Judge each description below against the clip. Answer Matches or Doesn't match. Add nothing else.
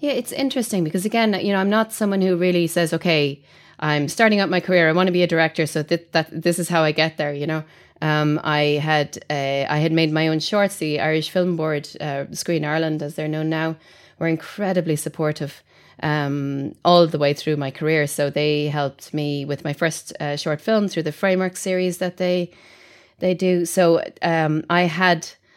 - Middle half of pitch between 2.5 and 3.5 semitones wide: Matches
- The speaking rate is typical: Doesn't match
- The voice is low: Doesn't match